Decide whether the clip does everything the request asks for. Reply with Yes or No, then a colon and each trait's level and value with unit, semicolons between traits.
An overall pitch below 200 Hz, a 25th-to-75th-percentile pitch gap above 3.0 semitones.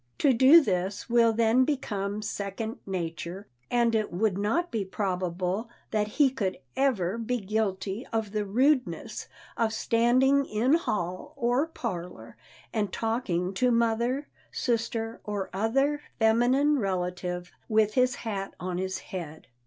No: high, 220 Hz; average, 4.3 semitones